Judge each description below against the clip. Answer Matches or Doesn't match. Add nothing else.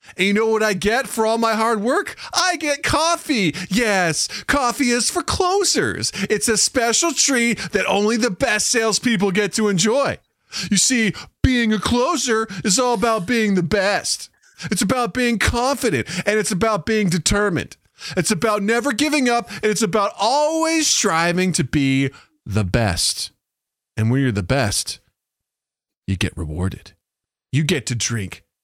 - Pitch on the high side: Matches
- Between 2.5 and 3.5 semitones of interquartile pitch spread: Doesn't match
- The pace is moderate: Matches